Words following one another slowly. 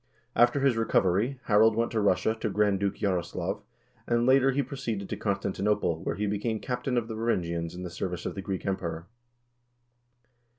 No: average, 175 wpm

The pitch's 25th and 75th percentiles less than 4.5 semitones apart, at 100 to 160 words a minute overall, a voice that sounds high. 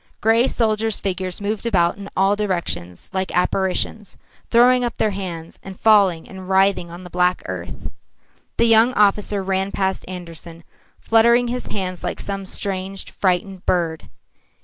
Yes: average, 2.8 semitones; average, 150 wpm; high, 195 Hz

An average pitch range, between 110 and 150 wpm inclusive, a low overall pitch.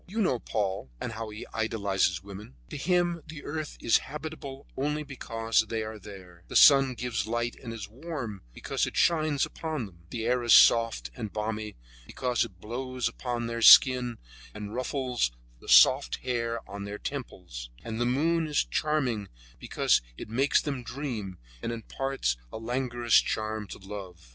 No: average, 4.3 semitones; average, 170 wpm; low, 115 Hz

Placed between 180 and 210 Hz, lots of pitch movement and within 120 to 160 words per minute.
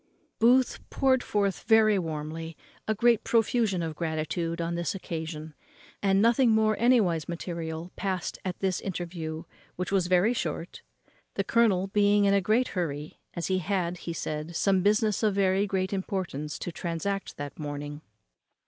No: medium, 185 Hz; average, 3.9 semitones; average, 155 wpm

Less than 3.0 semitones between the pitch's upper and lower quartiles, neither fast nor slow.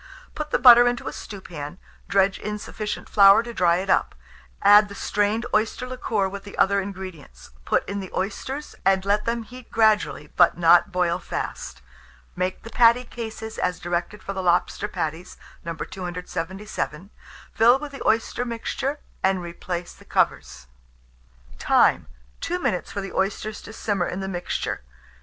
No: average, 3.7 semitones; average, 160 wpm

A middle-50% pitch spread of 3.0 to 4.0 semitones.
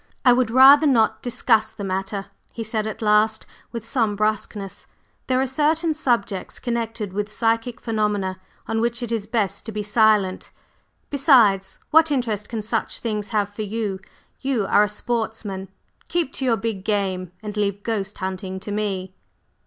No: narrow, 2.6 semitones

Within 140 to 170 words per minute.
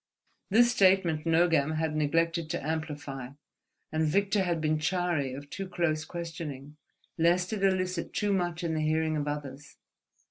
Yes: average, 150 wpm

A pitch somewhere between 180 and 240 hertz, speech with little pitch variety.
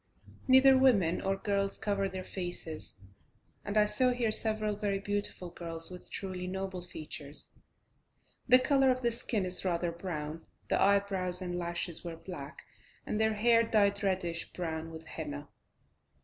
No: high, 190 Hz; average, 3.7 semitones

